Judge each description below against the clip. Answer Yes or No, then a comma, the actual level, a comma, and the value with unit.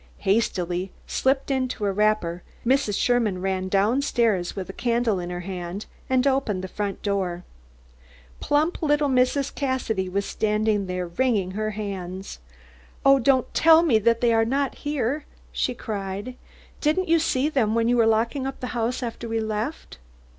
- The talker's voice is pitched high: Yes, high, 225 Hz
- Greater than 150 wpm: Yes, average, 165 wpm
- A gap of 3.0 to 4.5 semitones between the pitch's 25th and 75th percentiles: No, average, 5.1 semitones